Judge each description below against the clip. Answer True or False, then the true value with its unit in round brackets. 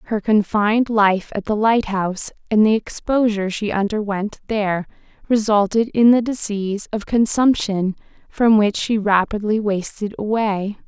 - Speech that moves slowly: True (130 wpm)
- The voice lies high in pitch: True (210 Hz)